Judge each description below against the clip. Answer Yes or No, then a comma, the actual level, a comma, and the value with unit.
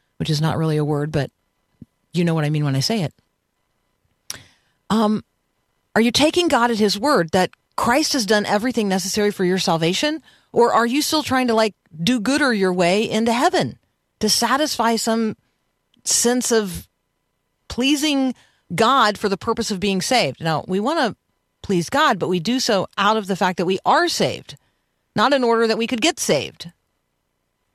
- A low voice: No, high, 215 Hz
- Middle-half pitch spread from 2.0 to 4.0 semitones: No, average, 5.1 semitones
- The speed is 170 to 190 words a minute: Yes, average, 185 wpm